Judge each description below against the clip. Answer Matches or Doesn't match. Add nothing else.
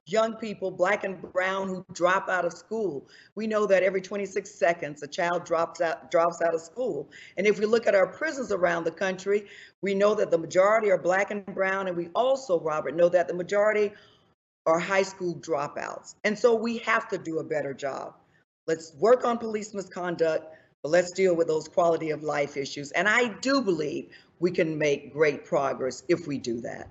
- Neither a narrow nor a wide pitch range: Matches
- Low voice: Doesn't match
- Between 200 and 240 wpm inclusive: Matches